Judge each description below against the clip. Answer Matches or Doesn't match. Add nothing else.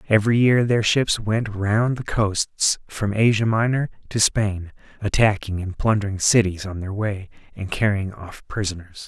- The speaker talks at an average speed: Matches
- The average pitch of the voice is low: Matches